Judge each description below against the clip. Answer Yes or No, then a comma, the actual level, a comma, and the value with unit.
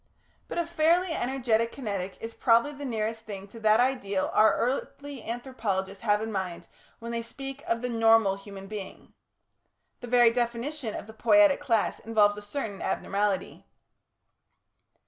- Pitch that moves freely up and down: No, average, 3.8 semitones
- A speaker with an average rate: Yes, average, 150 wpm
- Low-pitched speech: No, high, 230 Hz